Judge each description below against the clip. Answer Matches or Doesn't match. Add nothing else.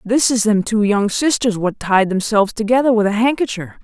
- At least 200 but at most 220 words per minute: Matches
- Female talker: Matches